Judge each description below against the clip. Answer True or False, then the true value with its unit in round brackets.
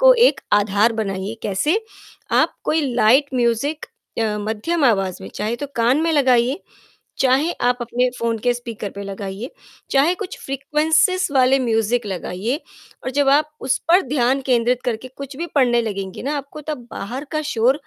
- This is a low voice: False (250 Hz)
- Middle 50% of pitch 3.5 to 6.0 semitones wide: True (4.2 semitones)